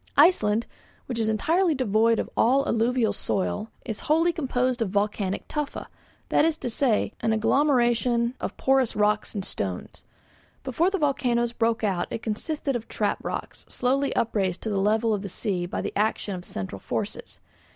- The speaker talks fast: No, average, 165 wpm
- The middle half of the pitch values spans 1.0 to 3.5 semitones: No, average, 4.1 semitones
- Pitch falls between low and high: No, high, 230 Hz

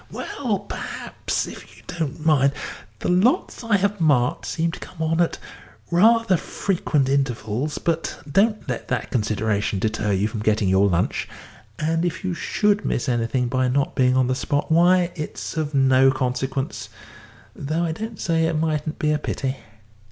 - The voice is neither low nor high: Yes, medium, 150 Hz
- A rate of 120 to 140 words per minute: No, average, 165 wpm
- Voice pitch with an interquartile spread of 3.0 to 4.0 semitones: No, average, 5.2 semitones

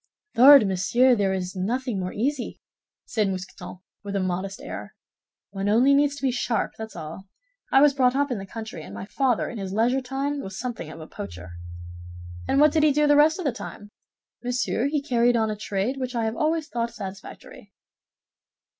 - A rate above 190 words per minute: Yes, average, 200 wpm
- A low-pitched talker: No, high, 235 Hz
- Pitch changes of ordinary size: No, wide, 5.7 semitones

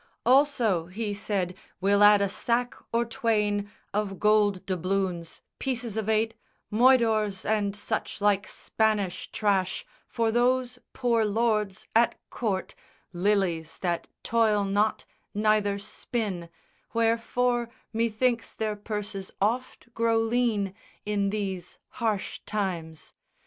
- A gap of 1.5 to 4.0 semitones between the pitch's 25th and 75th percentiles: Yes, narrow, 2.6 semitones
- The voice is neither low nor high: No, high, 210 Hz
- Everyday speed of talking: No, slow, 115 wpm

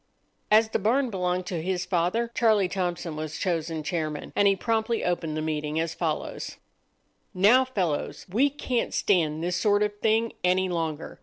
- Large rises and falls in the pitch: No, average, 4.8 semitones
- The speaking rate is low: No, average, 165 wpm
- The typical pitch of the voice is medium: Yes, medium, 180 Hz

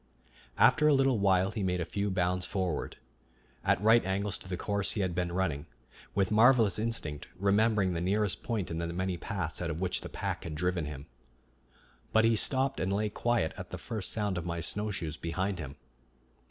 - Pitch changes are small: No, average, 3.4 semitones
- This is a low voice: Yes, very low, 95 Hz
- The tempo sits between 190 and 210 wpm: Yes, average, 195 wpm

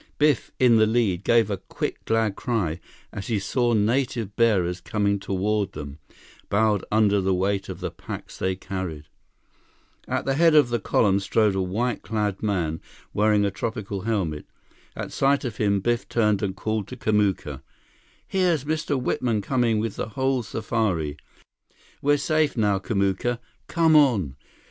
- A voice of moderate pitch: No, low, 105 Hz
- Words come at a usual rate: Yes, average, 160 wpm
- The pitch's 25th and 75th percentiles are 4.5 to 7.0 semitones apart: No, average, 3.7 semitones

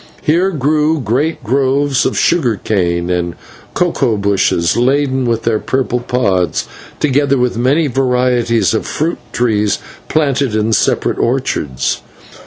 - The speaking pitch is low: Yes, low, 125 Hz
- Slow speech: Yes, slow, 125 wpm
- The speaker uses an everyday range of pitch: Yes, average, 4.5 semitones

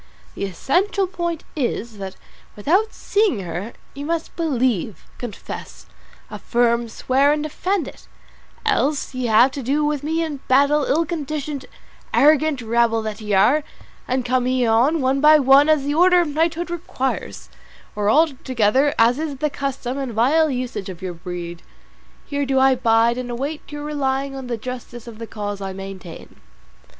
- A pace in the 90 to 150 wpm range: No, average, 165 wpm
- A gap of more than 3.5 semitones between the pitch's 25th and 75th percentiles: Yes, average, 4.7 semitones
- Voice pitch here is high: Yes, very high, 265 Hz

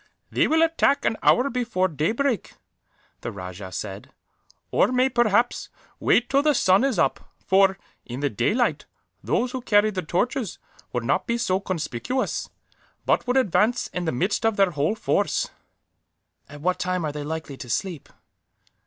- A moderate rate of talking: Yes, average, 160 wpm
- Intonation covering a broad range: Yes, wide, 8.3 semitones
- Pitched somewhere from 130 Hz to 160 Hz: No, high, 195 Hz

